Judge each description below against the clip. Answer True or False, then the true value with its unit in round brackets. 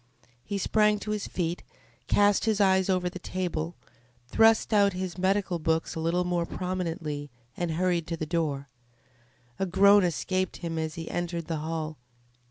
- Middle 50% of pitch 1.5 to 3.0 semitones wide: True (2.7 semitones)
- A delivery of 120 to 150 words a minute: False (165 wpm)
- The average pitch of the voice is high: False (175 Hz)